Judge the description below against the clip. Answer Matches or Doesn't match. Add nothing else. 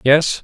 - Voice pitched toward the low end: Doesn't match